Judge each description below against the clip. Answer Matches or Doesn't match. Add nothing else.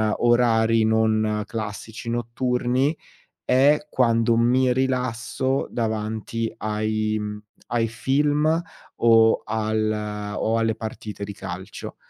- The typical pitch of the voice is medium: Doesn't match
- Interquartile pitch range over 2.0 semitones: Matches